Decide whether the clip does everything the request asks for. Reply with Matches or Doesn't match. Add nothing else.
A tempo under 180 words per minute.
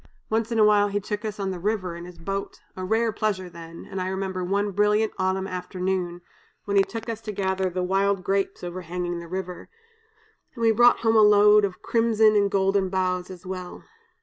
Doesn't match